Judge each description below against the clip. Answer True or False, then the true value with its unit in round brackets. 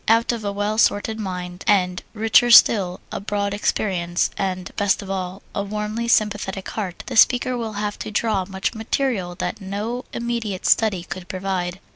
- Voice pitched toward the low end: False (205 Hz)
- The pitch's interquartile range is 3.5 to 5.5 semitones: False (2.8 semitones)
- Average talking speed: True (170 wpm)